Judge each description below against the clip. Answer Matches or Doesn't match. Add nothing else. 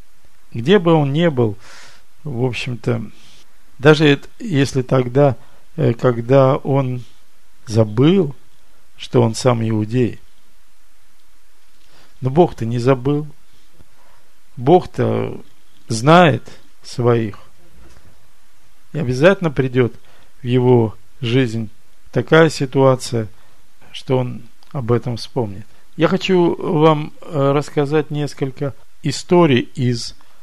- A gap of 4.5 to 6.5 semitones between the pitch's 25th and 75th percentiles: Doesn't match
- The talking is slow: Matches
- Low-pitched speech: Matches